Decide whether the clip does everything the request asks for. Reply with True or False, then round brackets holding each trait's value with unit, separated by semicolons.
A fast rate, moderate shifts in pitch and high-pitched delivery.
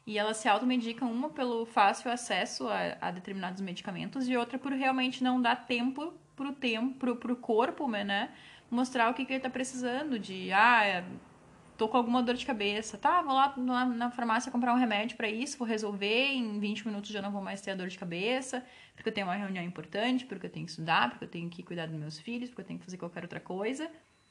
True (230 wpm; 4.0 semitones; 235 Hz)